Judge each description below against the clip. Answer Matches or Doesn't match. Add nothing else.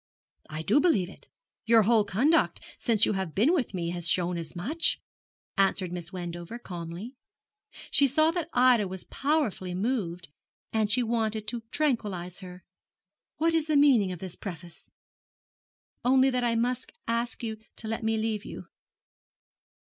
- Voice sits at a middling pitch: Doesn't match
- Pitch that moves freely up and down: Matches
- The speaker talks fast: Doesn't match